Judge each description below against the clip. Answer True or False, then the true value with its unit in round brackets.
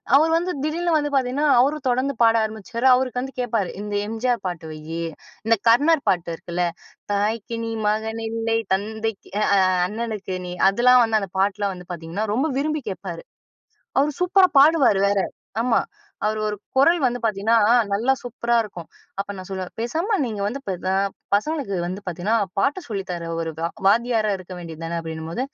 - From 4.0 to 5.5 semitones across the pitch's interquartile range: True (4.9 semitones)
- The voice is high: True (220 Hz)